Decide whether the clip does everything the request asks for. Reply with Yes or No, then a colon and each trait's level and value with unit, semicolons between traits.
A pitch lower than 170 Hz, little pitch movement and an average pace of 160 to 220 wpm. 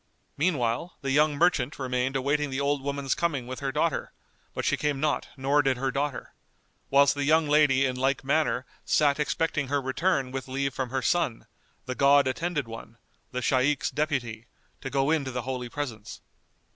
Yes: low, 135 Hz; narrow, 2.2 semitones; average, 185 wpm